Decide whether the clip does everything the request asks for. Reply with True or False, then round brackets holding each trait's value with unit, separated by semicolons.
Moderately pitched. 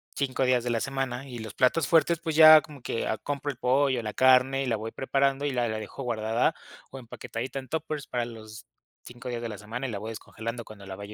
False (125 Hz)